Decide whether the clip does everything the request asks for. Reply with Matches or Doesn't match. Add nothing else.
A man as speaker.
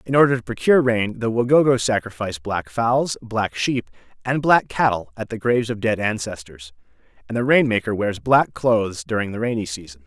Matches